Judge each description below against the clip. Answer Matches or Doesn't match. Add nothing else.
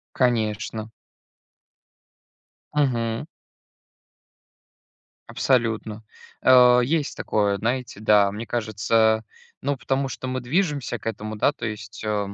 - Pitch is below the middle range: Matches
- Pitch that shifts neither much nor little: Matches